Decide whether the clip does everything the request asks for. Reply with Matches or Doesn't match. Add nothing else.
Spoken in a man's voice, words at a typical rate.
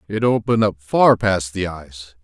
Matches